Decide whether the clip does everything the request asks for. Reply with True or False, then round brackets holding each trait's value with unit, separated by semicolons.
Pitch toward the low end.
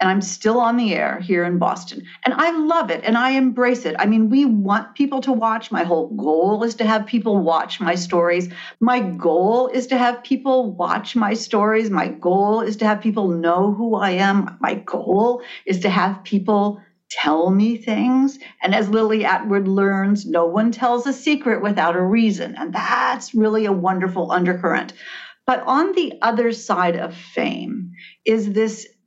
False (215 Hz)